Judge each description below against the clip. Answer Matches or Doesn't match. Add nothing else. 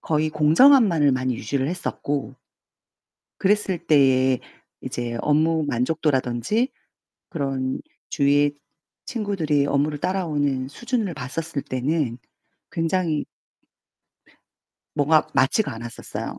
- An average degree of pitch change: Matches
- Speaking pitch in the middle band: Matches